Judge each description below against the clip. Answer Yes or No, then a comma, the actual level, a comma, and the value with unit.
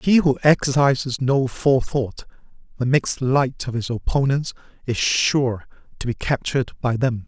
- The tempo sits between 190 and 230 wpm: No, average, 150 wpm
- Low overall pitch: Yes, low, 130 Hz